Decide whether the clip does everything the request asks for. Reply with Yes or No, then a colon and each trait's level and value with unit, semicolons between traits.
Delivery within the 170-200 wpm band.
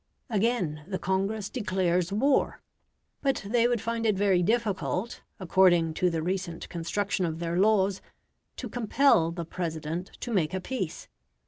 No: average, 145 wpm